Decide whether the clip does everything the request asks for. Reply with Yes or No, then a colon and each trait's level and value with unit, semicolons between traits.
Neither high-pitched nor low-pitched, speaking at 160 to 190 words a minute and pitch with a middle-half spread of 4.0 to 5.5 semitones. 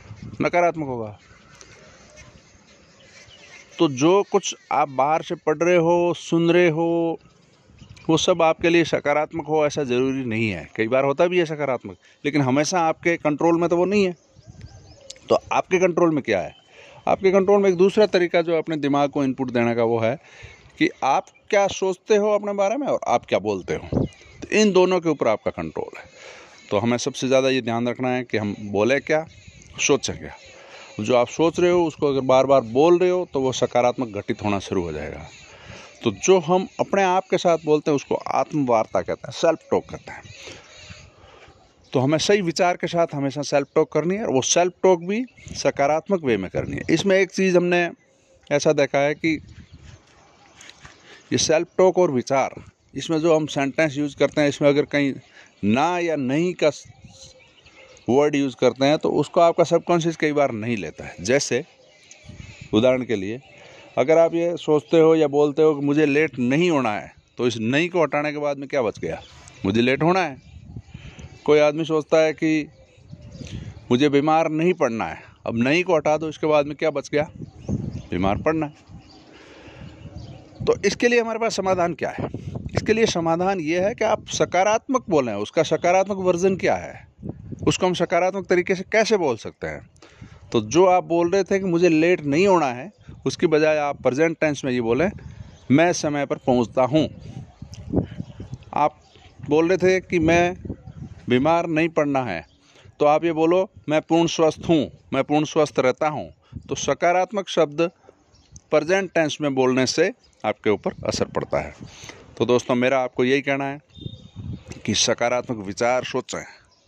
Yes: medium, 155 Hz; average, 180 wpm; average, 5.2 semitones